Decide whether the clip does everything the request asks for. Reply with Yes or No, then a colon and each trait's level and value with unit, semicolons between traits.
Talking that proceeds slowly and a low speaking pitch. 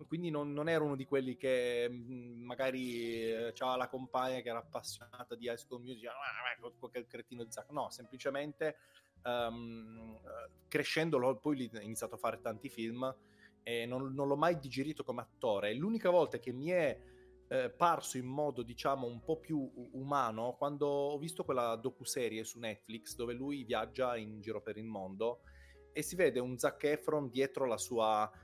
No: fast, 170 wpm; low, 125 Hz